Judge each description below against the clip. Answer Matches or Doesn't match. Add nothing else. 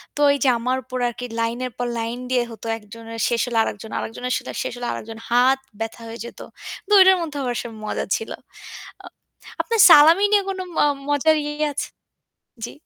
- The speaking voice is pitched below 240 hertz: Doesn't match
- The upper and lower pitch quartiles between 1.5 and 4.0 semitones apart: Doesn't match